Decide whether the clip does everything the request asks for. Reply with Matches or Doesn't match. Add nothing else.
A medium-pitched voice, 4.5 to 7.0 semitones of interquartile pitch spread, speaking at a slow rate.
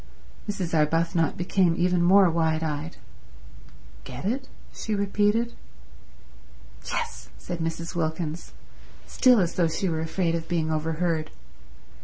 Doesn't match